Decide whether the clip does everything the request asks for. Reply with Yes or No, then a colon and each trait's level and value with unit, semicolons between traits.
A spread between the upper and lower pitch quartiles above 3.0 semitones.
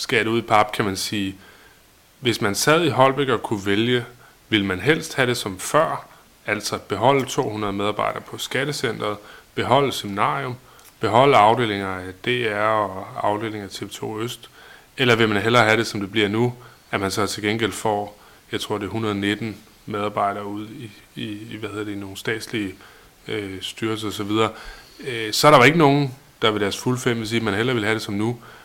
No: narrow, 2.6 semitones